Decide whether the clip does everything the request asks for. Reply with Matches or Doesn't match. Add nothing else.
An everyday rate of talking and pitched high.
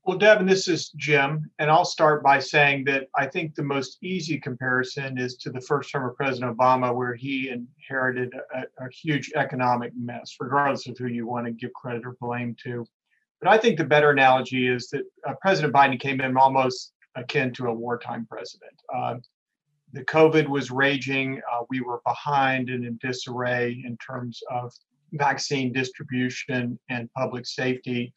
Doesn't match